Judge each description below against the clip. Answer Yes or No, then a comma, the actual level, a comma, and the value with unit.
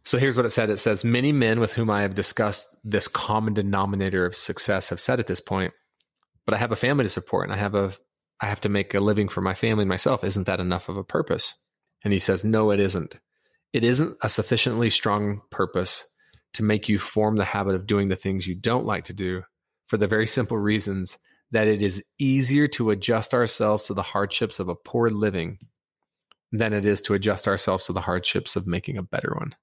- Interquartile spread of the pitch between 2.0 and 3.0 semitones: Yes, narrow, 2.5 semitones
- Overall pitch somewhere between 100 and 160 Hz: Yes, low, 105 Hz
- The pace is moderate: No, fast, 225 wpm